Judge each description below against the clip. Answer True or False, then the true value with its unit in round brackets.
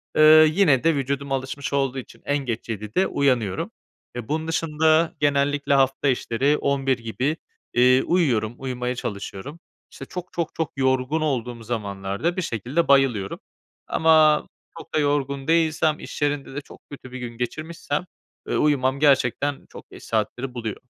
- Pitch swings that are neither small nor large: True (3.7 semitones)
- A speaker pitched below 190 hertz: True (140 Hz)